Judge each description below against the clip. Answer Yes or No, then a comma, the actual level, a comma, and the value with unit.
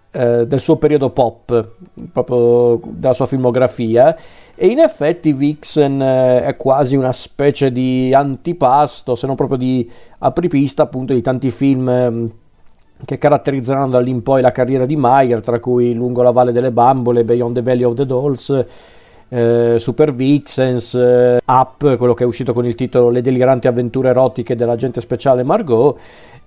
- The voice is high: No, low, 130 Hz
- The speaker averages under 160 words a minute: Yes, average, 145 wpm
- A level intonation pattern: Yes, narrow, 1.9 semitones